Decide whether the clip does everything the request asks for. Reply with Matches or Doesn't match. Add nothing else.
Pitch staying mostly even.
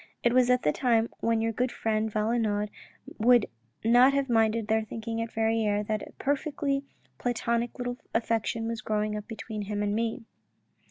Matches